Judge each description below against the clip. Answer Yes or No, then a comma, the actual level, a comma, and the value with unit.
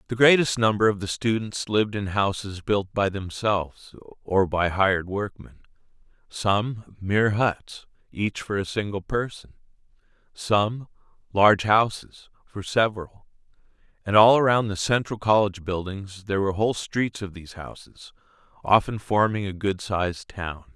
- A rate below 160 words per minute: Yes, average, 140 wpm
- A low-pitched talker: Yes, low, 100 Hz